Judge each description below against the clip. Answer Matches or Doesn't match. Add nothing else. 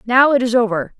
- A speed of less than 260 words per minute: Matches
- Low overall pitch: Doesn't match